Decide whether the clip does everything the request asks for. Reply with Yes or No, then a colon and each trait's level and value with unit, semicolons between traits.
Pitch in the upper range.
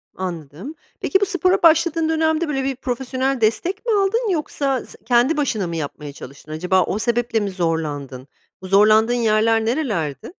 Yes: high, 235 Hz